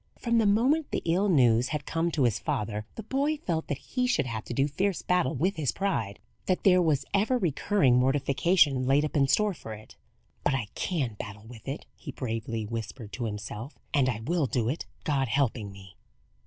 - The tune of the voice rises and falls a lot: Yes, wide, 7.8 semitones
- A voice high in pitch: No, medium, 140 Hz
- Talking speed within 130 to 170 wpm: No, fast, 205 wpm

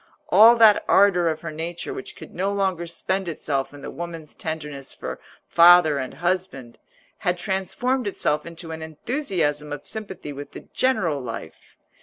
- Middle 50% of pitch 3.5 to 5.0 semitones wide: Yes, average, 4.6 semitones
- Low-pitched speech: No, medium, 170 Hz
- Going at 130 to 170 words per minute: Yes, average, 160 wpm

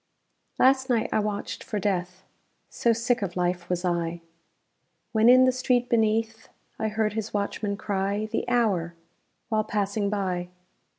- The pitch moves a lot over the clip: No, average, 3.2 semitones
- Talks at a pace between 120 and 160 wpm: Yes, average, 150 wpm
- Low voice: No, high, 210 Hz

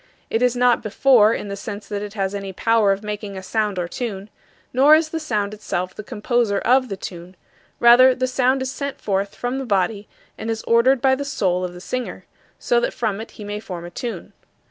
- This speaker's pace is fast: Yes, fast, 225 wpm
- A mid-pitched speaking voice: No, high, 215 Hz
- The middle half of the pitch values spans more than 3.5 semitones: Yes, average, 4.2 semitones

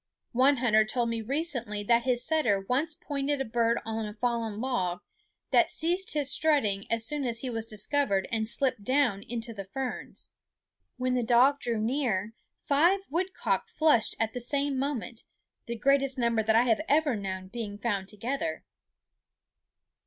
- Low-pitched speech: No, high, 240 Hz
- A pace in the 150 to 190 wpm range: Yes, average, 160 wpm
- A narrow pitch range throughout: No, average, 4.1 semitones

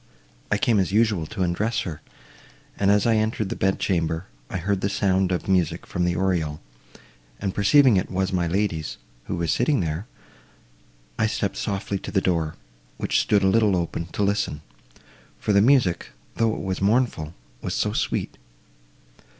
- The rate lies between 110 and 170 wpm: Yes, average, 165 wpm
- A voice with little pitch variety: No, average, 3.3 semitones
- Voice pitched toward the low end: Yes, very low, 95 Hz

